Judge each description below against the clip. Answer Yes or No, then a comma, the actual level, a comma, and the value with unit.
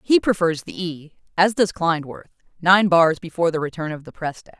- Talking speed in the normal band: Yes, average, 170 wpm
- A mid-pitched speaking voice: Yes, medium, 170 Hz